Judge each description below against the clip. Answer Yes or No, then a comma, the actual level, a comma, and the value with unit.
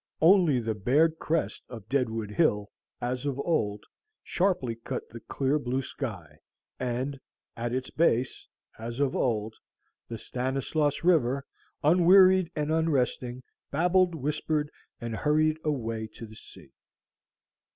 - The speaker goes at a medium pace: No, slow, 125 wpm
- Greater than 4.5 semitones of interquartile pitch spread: Yes, average, 5.2 semitones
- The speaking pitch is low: Yes, low, 130 Hz